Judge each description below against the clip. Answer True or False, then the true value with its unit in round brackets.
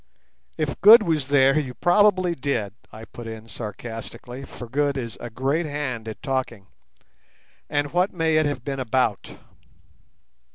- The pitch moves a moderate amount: True (4.6 semitones)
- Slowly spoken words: False (150 wpm)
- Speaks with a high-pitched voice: False (135 Hz)